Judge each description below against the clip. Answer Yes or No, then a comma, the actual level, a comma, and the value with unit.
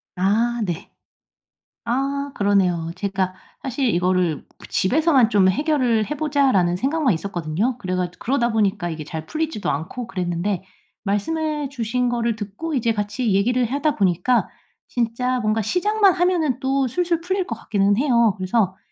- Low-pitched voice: No, high, 230 Hz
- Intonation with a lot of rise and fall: Yes, wide, 6.2 semitones